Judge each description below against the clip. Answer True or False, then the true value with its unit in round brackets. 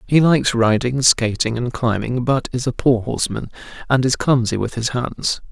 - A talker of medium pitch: False (125 Hz)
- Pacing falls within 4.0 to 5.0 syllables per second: True (4.9 syllables/s)